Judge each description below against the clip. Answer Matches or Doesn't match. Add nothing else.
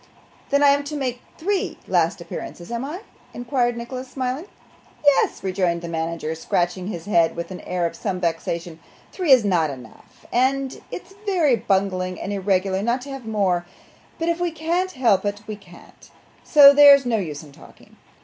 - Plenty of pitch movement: Matches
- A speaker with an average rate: Matches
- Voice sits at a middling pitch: Doesn't match